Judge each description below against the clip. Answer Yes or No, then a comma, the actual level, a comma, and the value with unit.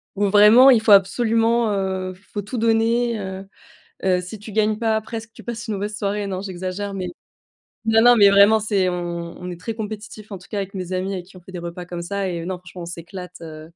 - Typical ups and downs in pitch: Yes, average, 3.0 semitones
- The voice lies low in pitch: No, high, 200 Hz